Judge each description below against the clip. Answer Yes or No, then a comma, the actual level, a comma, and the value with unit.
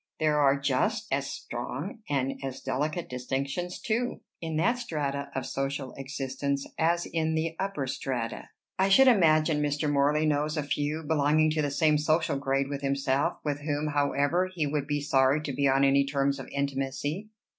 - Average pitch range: No, narrow, 2.3 semitones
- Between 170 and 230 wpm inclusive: Yes, average, 175 wpm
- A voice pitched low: No, medium, 145 Hz